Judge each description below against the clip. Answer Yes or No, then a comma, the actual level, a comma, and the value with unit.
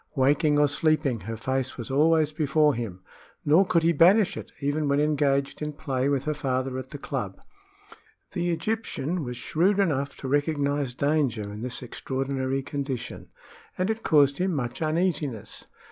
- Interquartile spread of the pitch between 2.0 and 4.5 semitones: Yes, average, 3.0 semitones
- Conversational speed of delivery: Yes, average, 160 wpm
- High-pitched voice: No, medium, 145 Hz